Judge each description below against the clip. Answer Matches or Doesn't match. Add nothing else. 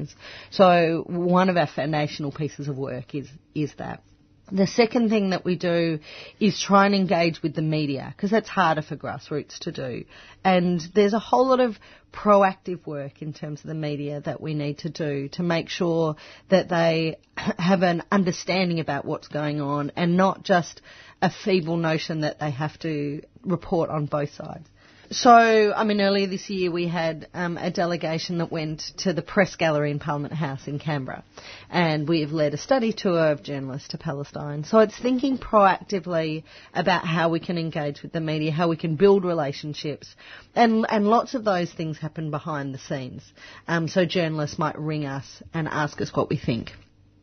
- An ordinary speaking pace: Matches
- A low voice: Doesn't match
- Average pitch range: Matches